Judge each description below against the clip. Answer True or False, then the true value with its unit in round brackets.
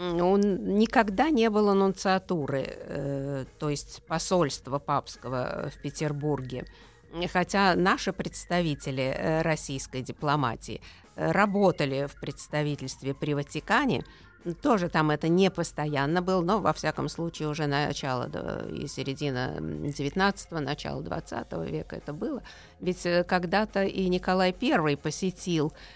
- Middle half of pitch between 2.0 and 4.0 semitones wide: False (4.6 semitones)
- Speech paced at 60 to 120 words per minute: True (115 wpm)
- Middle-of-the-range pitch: True (155 Hz)